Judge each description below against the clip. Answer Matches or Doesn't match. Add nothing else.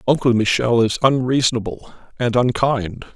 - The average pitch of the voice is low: Matches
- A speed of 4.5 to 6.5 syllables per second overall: Matches